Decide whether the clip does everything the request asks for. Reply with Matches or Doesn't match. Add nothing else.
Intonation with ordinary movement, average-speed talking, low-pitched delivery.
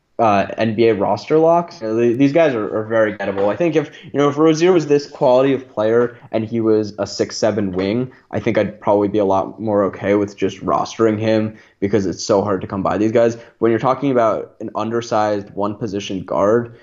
Doesn't match